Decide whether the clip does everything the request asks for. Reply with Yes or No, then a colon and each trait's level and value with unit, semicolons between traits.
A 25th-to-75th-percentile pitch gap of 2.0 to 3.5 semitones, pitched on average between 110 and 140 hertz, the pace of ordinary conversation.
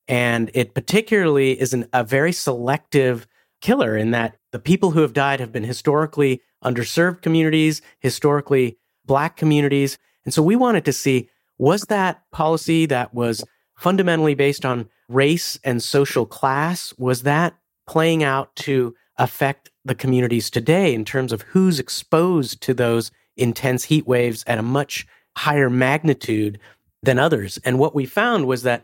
No: average, 4.1 semitones; low, 135 Hz; average, 155 wpm